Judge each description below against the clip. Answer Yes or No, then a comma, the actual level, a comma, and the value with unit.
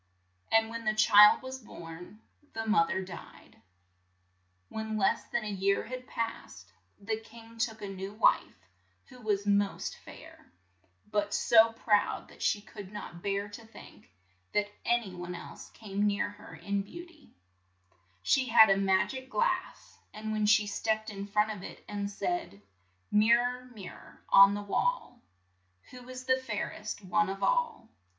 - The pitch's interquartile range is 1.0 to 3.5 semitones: Yes, narrow, 2.5 semitones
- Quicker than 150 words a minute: Yes, average, 170 wpm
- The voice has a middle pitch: No, high, 210 Hz